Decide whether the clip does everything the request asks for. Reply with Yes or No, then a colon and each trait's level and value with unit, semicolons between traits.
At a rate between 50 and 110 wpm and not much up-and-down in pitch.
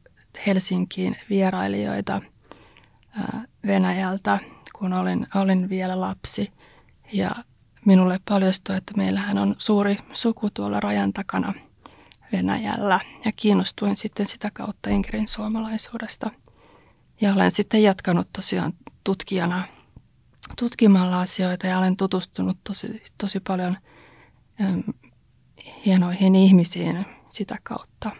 Yes: average, 100 wpm; narrow, 2.3 semitones